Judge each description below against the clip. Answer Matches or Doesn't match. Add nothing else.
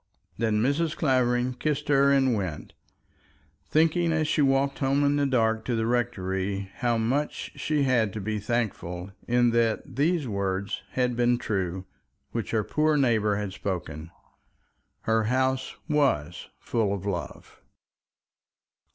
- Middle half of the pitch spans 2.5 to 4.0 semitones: Doesn't match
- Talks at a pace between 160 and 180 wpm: Doesn't match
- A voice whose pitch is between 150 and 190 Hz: Doesn't match